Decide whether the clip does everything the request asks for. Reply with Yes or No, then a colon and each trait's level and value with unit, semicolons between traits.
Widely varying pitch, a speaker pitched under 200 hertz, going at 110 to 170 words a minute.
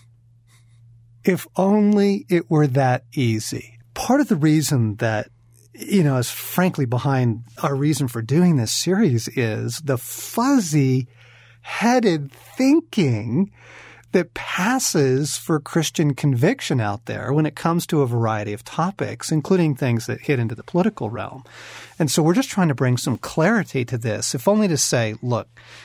Yes: wide, 6.3 semitones; low, 135 Hz; average, 155 wpm